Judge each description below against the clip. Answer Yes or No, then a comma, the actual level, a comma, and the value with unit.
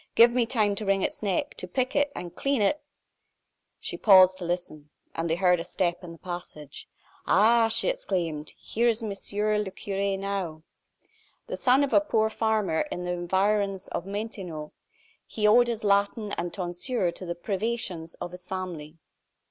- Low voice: No, high, 195 Hz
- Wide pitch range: No, average, 3.9 semitones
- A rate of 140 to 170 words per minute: No, average, 180 wpm